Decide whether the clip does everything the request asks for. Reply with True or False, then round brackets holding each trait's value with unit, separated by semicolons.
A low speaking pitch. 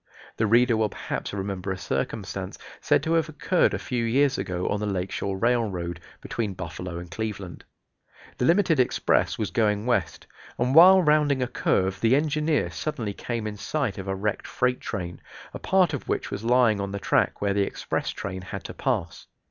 True (110 Hz)